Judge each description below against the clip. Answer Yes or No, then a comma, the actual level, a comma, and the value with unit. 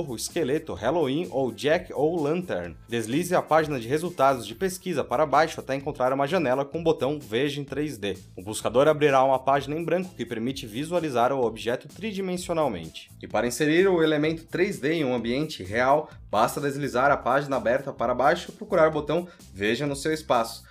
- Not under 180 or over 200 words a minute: Yes, fast, 185 wpm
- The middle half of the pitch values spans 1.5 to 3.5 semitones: No, average, 4.9 semitones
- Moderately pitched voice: Yes, medium, 145 Hz